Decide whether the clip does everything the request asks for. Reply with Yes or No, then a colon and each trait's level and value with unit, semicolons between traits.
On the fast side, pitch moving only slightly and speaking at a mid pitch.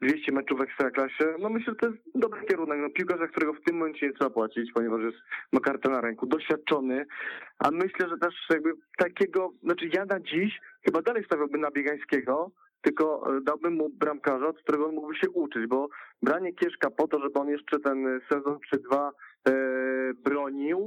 No: fast, 185 wpm; average, 3.8 semitones; medium, 150 Hz